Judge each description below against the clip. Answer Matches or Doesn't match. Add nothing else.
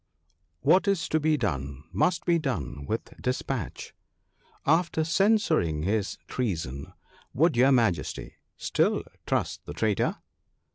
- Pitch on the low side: Matches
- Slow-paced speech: Matches